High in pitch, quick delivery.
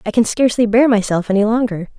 Yes: high, 220 Hz; fast, 210 wpm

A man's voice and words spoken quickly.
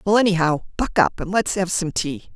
No: female; fast, 230 wpm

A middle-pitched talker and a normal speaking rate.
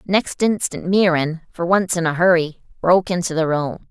Yes: medium, 175 Hz; average, 185 wpm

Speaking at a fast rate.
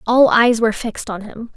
Yes: fast, 230 wpm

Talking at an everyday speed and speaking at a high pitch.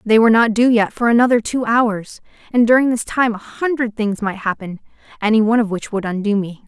No: fast, 225 wpm; high, 225 Hz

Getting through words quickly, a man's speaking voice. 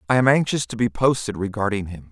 Yes: fast, 225 wpm; male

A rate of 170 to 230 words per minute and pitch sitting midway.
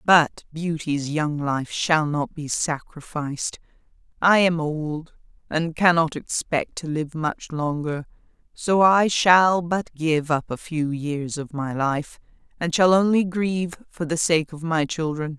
No: average, 155 wpm; medium, 160 Hz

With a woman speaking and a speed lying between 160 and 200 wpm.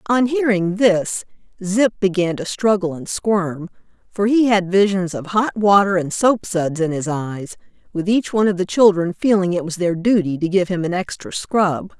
Yes: female; average, 190 wpm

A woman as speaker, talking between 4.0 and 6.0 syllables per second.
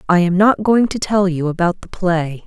Yes: female; 4.8 syllables/s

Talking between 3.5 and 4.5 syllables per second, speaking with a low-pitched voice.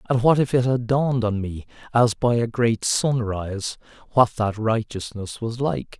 Yes: 4.4 syllables/s; low, 115 Hz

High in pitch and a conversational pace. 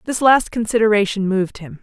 Yes: high, 210 Hz; average, 165 wpm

